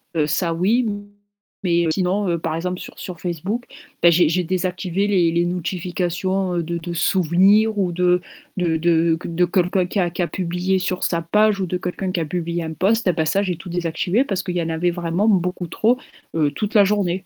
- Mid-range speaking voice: Yes, medium, 180 Hz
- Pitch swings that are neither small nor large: No, narrow, 2.0 semitones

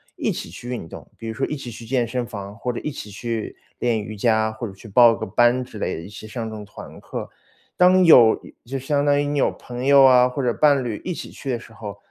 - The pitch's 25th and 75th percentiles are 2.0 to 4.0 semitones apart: Yes, average, 3.5 semitones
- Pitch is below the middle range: Yes, low, 120 Hz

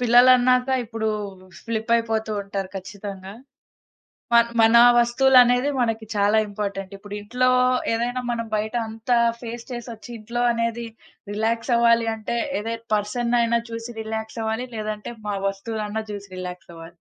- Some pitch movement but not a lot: No, narrow, 2.3 semitones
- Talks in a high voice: Yes, high, 225 Hz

